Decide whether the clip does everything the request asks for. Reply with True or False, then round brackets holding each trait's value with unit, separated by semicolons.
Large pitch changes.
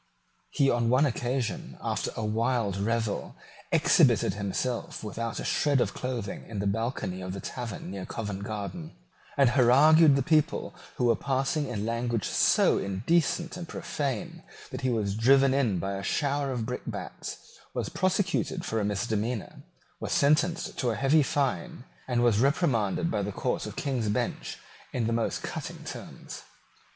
False (4.7 semitones)